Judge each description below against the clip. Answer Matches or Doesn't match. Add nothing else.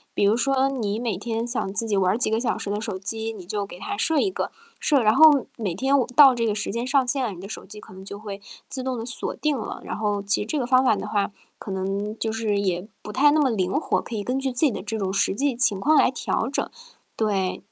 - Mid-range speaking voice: Doesn't match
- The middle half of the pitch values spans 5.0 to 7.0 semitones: Doesn't match